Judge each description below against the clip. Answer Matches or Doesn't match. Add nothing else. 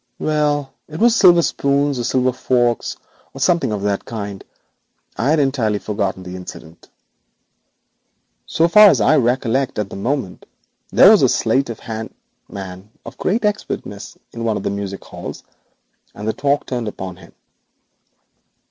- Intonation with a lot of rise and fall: Matches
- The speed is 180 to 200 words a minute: Doesn't match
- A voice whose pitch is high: Doesn't match